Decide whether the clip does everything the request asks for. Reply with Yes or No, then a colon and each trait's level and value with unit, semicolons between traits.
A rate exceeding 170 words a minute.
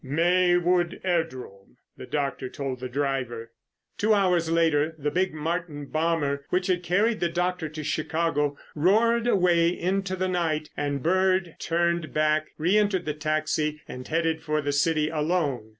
No: average, 150 wpm